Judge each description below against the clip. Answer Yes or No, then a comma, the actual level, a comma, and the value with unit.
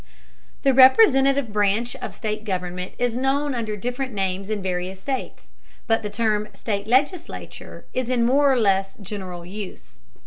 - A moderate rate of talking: Yes, average, 150 wpm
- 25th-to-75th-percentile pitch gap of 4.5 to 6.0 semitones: Yes, average, 4.9 semitones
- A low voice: No, high, 220 Hz